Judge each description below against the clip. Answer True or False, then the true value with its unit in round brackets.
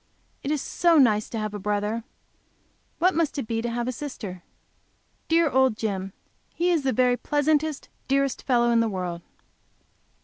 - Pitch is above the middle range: True (245 Hz)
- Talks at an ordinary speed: True (175 wpm)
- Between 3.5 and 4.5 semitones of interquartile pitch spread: False (5.4 semitones)